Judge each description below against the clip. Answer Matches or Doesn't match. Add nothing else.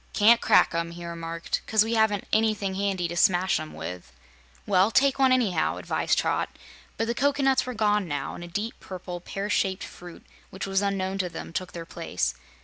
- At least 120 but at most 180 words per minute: Doesn't match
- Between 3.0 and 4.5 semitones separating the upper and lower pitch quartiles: Matches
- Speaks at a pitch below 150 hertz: Doesn't match